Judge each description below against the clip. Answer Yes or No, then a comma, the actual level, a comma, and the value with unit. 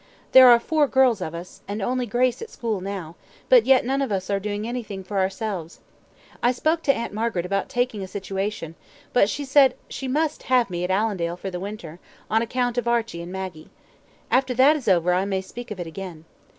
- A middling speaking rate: No, fast, 215 wpm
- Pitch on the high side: Yes, high, 210 Hz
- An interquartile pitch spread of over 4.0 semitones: Yes, average, 5.0 semitones